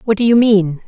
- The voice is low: No, high, 210 Hz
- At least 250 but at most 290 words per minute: Yes, fast, 275 wpm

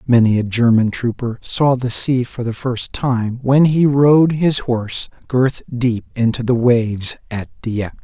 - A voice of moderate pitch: No, low, 120 Hz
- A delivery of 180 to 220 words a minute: No, average, 170 wpm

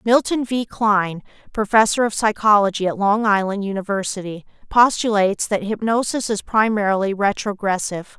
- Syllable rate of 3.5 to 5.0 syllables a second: No, 5.3 syllables/s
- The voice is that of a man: No, female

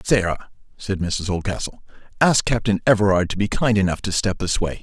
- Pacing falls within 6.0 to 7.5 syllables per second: No, 5.4 syllables/s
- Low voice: Yes, low, 100 Hz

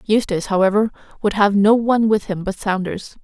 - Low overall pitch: No, high, 205 Hz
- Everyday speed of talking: Yes, average, 185 wpm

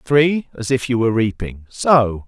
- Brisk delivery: No, average, 160 wpm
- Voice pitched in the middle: No, low, 120 Hz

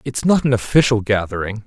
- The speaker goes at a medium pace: Yes, average, 180 wpm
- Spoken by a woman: No, male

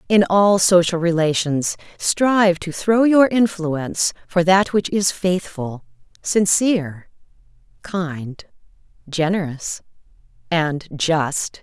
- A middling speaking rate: No, slow, 100 wpm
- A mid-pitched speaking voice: Yes, medium, 175 Hz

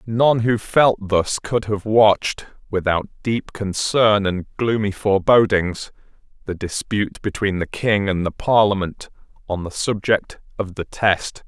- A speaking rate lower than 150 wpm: Yes, average, 140 wpm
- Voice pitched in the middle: No, low, 100 Hz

